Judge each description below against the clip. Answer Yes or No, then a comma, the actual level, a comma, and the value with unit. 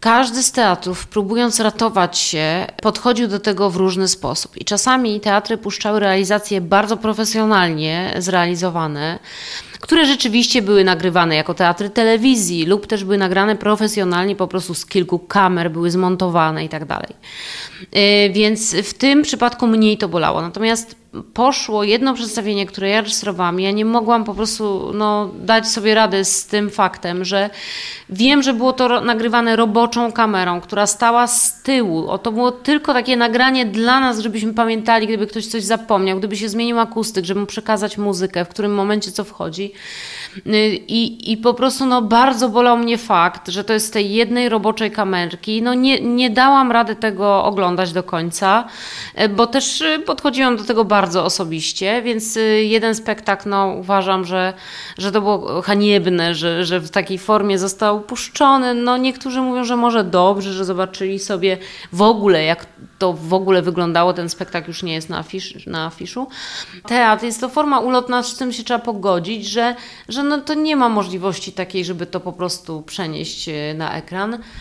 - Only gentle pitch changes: No, average, 3.8 semitones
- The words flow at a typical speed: No, fast, 165 wpm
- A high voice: Yes, high, 210 Hz